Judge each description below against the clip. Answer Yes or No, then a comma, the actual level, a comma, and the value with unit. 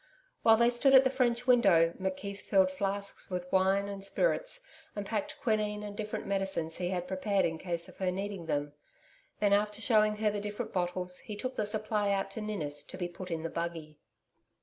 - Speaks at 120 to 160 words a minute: No, average, 200 wpm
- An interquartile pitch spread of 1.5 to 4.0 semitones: Yes, average, 2.9 semitones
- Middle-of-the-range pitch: No, high, 200 Hz